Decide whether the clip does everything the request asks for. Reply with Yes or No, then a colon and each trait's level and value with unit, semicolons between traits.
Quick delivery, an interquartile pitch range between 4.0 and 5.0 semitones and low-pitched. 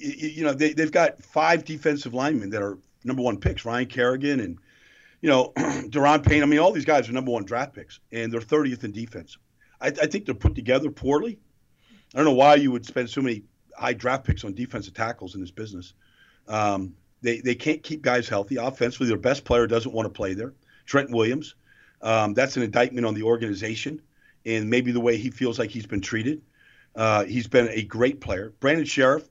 Yes: fast, 210 wpm; average, 4.3 semitones; low, 120 Hz